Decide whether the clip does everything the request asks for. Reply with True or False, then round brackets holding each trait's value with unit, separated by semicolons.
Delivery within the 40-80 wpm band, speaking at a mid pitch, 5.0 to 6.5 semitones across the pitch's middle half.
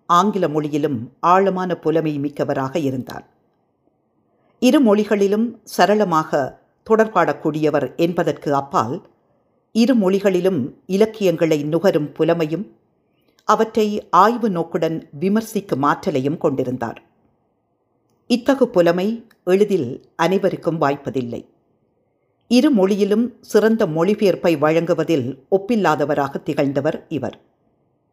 True (75 wpm; 180 Hz; 5.3 semitones)